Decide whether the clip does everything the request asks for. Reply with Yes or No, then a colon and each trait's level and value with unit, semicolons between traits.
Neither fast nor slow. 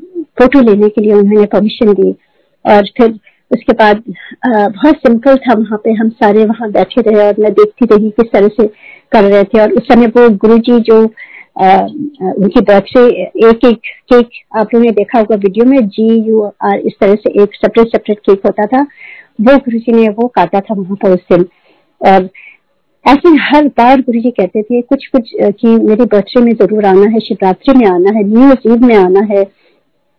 No: fast, 195 wpm